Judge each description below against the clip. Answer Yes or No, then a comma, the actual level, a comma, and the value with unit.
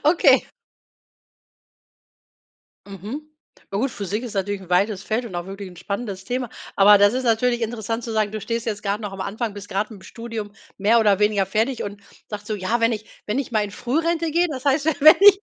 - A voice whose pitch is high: Yes, high, 215 Hz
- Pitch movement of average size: Yes, average, 3.3 semitones